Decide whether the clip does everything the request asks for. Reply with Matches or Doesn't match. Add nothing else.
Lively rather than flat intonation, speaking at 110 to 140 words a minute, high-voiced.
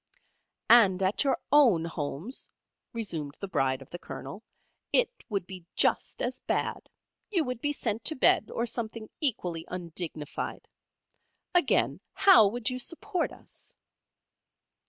Matches